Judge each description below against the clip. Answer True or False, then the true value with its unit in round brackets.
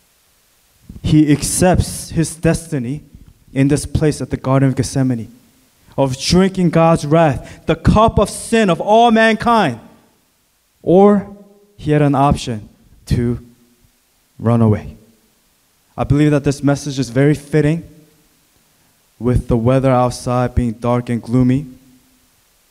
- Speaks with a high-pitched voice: False (140 Hz)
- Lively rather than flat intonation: False (5.0 semitones)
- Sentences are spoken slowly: True (125 wpm)